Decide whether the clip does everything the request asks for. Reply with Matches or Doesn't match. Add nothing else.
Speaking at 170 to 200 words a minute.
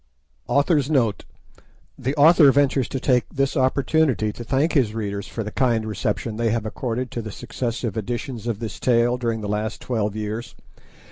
Matches